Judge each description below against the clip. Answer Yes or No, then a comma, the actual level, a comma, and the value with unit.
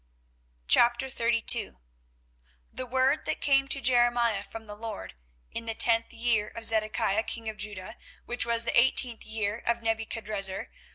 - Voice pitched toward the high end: Yes, high, 230 Hz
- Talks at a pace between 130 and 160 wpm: Yes, average, 140 wpm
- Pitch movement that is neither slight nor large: No, narrow, 1.8 semitones